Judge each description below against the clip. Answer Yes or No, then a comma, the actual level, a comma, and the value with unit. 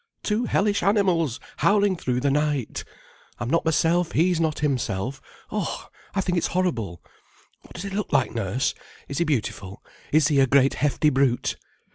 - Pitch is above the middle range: No, medium, 150 Hz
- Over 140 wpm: Yes, average, 165 wpm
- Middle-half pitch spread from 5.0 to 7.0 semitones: Yes, wide, 5.4 semitones